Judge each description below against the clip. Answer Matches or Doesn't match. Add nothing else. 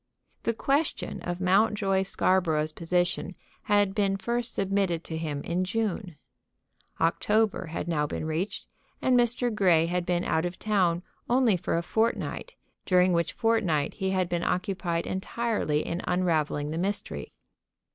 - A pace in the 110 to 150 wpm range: Matches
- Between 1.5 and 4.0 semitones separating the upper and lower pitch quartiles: Matches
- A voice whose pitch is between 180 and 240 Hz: Matches